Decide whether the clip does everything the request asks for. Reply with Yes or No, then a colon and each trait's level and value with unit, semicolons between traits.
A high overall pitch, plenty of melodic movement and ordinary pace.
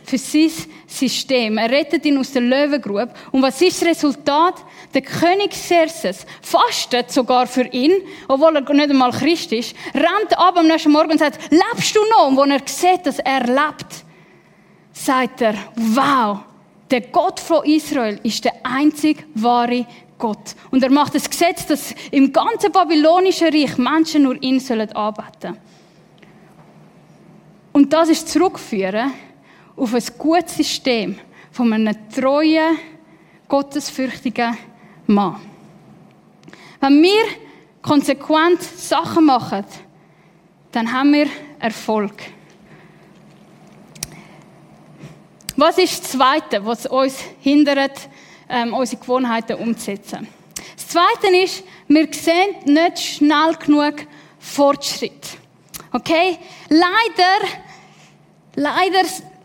No: very high, 275 Hz; wide, 5.7 semitones; slow, 115 wpm